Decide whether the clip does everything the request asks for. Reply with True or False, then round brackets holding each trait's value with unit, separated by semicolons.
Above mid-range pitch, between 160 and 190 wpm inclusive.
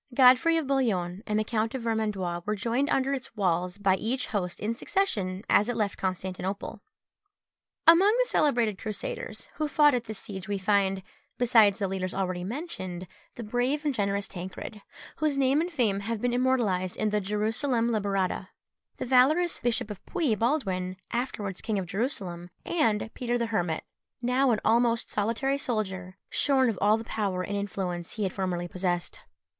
True (215 Hz; 170 wpm)